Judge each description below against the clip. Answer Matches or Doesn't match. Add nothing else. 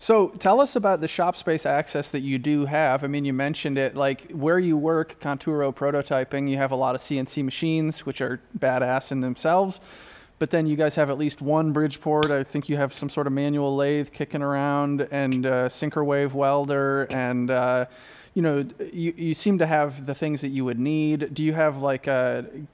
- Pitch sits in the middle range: Matches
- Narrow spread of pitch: Matches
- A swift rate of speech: Matches